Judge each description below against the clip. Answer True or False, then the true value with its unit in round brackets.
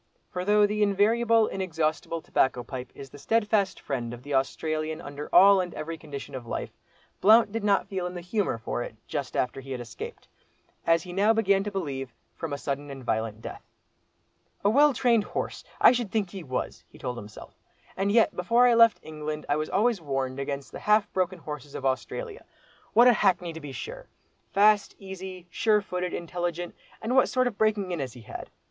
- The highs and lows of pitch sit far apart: True (6.8 semitones)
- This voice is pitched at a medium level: True (180 Hz)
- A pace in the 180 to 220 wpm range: True (200 wpm)